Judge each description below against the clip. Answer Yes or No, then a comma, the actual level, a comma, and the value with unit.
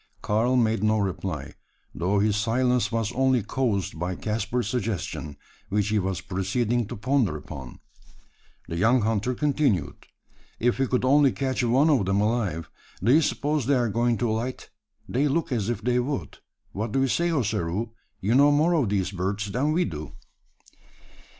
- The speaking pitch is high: No, low, 115 Hz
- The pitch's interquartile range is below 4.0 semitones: No, average, 4.4 semitones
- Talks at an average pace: Yes, average, 170 wpm